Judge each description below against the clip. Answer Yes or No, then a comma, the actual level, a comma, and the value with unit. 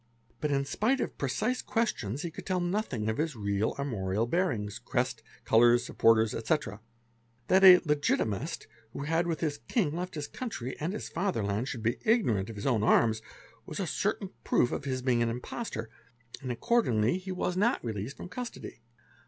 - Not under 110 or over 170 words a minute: No, average, 185 wpm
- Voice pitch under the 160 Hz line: Yes, low, 135 Hz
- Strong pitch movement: Yes, wide, 8.1 semitones